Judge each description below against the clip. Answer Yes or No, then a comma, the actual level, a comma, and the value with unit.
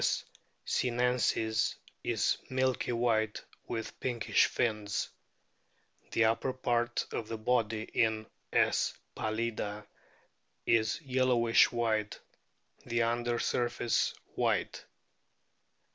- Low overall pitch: Yes, low, 115 Hz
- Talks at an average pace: No, slow, 85 wpm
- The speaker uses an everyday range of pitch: No, narrow, 1.7 semitones